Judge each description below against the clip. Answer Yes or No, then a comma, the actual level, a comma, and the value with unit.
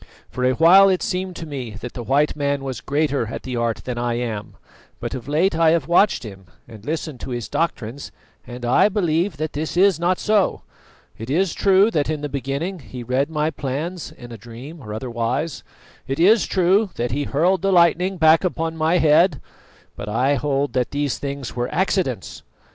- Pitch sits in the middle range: Yes, medium, 145 Hz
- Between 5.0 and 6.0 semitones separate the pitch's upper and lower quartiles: Yes, wide, 5.5 semitones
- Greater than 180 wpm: Yes, average, 200 wpm